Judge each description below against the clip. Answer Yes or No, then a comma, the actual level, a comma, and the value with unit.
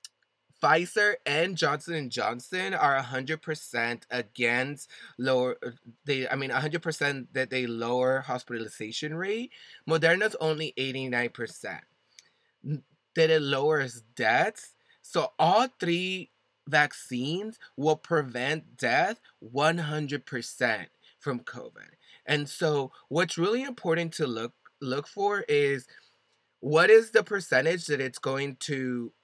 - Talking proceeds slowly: Yes, slow, 110 wpm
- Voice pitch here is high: No, medium, 145 Hz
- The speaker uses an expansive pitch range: No, average, 4.3 semitones